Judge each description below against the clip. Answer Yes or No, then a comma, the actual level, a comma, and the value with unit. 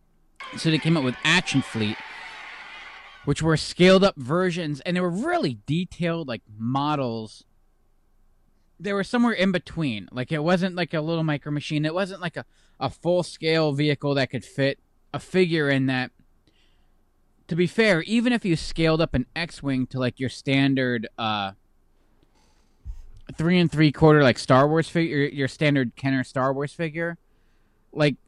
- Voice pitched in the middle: Yes, medium, 145 Hz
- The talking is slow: No, average, 165 wpm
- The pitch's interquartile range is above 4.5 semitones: Yes, average, 4.9 semitones